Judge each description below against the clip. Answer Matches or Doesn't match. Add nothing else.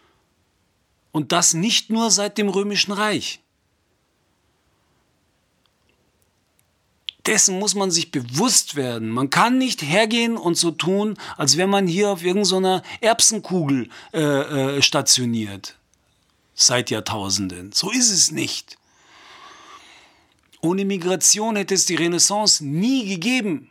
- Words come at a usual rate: Doesn't match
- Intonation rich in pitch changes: Matches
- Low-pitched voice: Doesn't match